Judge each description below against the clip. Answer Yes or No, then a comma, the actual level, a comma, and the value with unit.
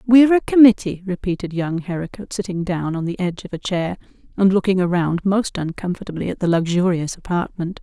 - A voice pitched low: No, medium, 185 Hz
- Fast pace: No, average, 175 wpm